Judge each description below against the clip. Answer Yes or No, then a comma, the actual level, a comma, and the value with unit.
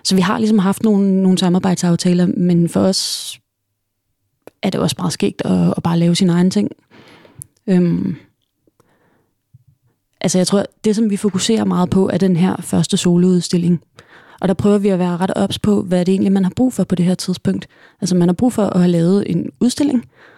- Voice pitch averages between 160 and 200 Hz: Yes, medium, 185 Hz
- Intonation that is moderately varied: No, narrow, 2.3 semitones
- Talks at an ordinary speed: Yes, average, 200 wpm